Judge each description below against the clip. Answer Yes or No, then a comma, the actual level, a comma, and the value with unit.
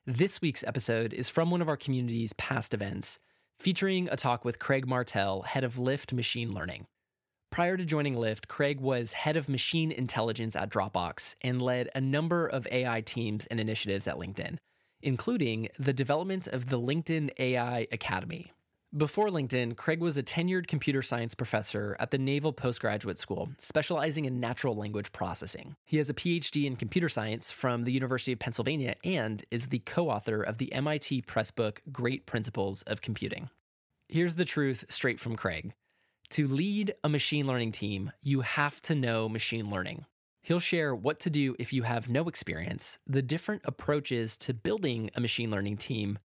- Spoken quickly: No, average, 175 wpm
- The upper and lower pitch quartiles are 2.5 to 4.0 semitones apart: No, average, 4.9 semitones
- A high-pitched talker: No, low, 125 Hz